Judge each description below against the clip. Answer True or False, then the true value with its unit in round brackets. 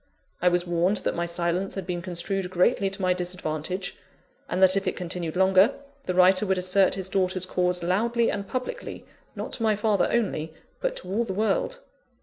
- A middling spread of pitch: False (1.9 semitones)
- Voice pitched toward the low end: False (185 Hz)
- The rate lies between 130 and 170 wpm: False (190 wpm)